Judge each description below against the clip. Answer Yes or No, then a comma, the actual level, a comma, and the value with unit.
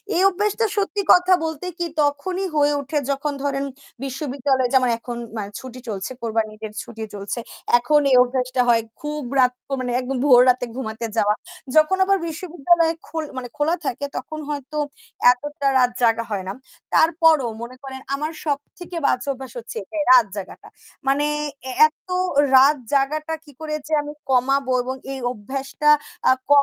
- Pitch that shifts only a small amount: No, average, 3.6 semitones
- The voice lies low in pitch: No, very high, 275 Hz